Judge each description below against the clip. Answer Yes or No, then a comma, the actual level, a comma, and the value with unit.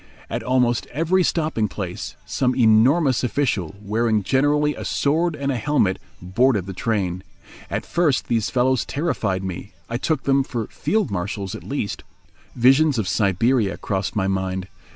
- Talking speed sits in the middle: Yes, average, 150 wpm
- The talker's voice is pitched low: Yes, low, 120 Hz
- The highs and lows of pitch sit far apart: Yes, wide, 6.0 semitones